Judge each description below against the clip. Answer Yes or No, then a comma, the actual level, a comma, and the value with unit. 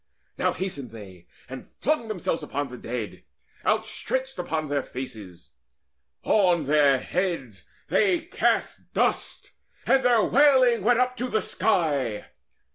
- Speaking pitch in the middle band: Yes, medium, 170 Hz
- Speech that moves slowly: Yes, slow, 125 wpm